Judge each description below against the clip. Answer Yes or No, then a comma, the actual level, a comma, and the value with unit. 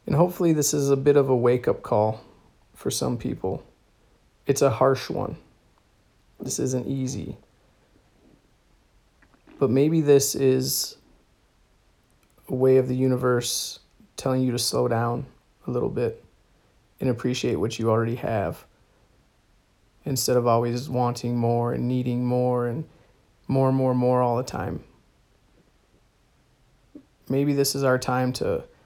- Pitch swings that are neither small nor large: No, narrow, 1.9 semitones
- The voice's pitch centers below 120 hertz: No, low, 125 Hz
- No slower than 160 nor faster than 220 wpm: No, slow, 135 wpm